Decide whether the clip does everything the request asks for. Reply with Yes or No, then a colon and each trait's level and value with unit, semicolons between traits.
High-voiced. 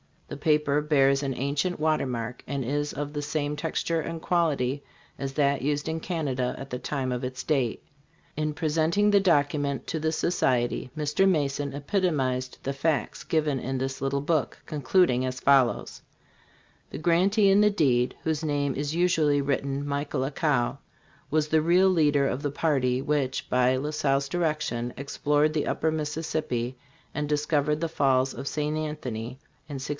No: medium, 145 Hz